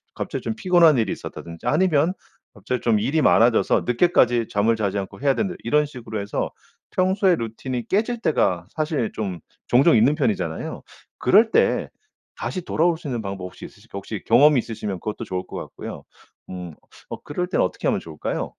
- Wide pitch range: Yes, wide, 7.7 semitones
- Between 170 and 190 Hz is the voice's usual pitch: No, low, 120 Hz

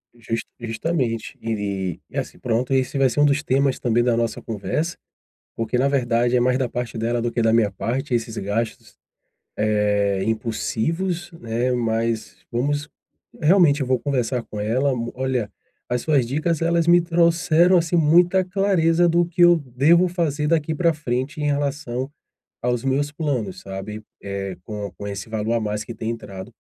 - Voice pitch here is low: Yes, low, 125 Hz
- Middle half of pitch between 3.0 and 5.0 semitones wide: No, wide, 5.6 semitones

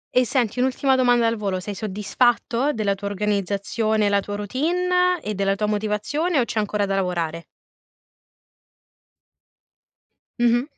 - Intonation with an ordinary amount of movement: Yes, average, 3.9 semitones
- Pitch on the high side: Yes, high, 215 Hz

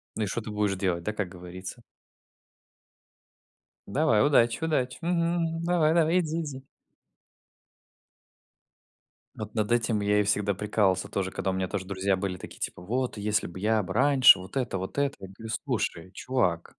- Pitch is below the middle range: Yes, low, 105 Hz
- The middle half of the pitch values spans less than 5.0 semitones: No, wide, 5.8 semitones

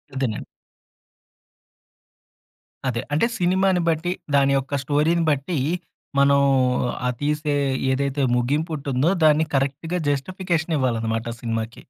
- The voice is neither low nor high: Yes, medium, 145 Hz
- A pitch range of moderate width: Yes, average, 3.4 semitones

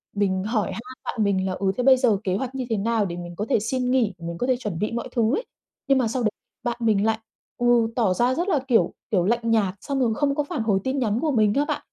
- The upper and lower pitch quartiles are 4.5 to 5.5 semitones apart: No, average, 3.9 semitones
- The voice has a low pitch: No, high, 225 Hz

